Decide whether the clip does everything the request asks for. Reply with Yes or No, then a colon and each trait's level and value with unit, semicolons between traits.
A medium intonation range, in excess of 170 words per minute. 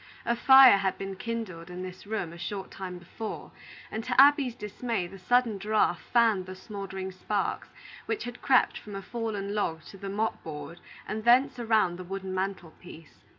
Yes: average, 3.6 semitones; average, 185 wpm